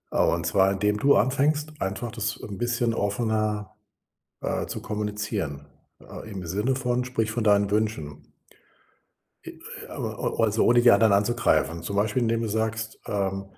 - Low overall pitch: Yes, low, 105 Hz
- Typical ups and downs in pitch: Yes, average, 3.0 semitones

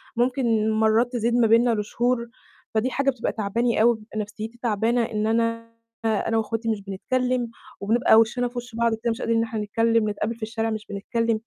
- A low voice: No, high, 225 Hz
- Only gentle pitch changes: Yes, narrow, 1.6 semitones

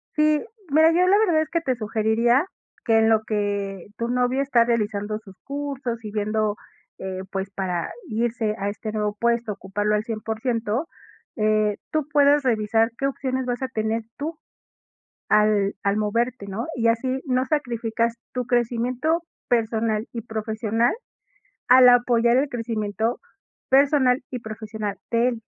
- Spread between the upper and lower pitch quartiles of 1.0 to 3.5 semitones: Yes, average, 3.0 semitones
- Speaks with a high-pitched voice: Yes, high, 230 Hz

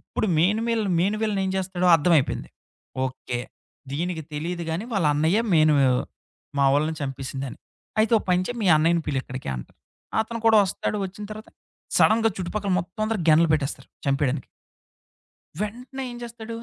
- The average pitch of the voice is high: No, medium, 175 Hz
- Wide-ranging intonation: Yes, wide, 6.3 semitones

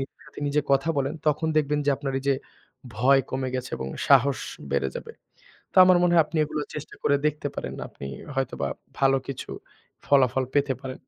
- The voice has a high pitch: No, medium, 140 Hz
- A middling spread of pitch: No, narrow, 2.2 semitones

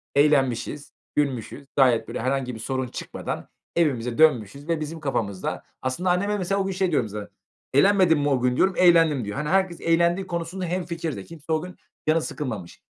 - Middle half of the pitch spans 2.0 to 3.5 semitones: No, average, 5.1 semitones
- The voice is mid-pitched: Yes, medium, 150 Hz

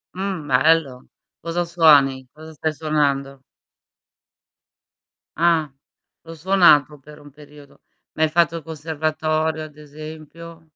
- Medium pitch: Yes, medium, 155 Hz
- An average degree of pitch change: No, narrow, 1.9 semitones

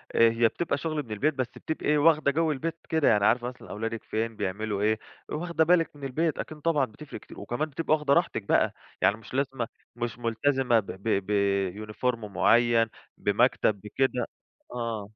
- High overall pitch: No, low, 120 Hz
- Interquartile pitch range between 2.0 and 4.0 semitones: No, wide, 5.5 semitones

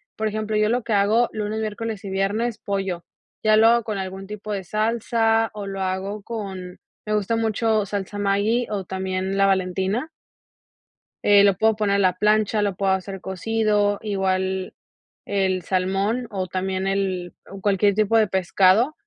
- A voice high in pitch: Yes, high, 200 Hz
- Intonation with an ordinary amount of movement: No, narrow, 2.2 semitones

